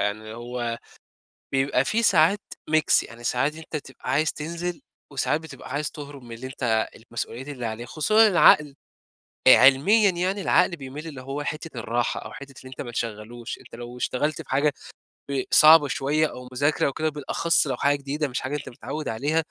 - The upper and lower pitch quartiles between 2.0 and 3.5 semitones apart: No, average, 3.9 semitones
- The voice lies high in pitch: No, medium, 140 Hz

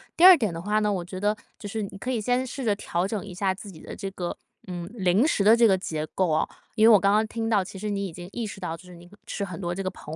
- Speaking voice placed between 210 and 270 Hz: No, high, 200 Hz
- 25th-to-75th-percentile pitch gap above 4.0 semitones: No, average, 3.2 semitones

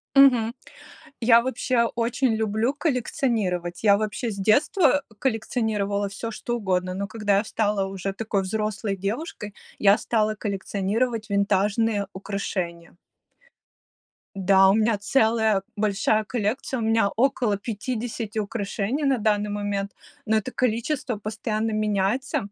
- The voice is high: Yes, high, 215 Hz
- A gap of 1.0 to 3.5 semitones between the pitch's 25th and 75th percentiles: Yes, average, 2.7 semitones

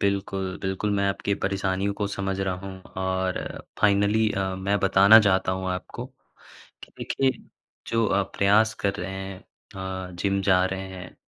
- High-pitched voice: No, very low, 95 Hz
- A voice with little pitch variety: Yes, narrow, 1.2 semitones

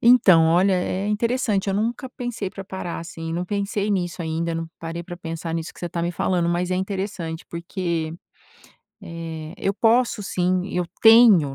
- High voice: No, medium, 180 Hz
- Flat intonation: No, average, 3.3 semitones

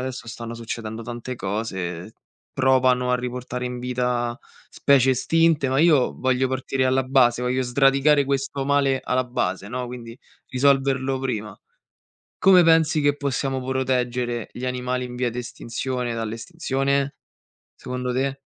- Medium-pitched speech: No, low, 125 Hz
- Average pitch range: No, narrow, 1.9 semitones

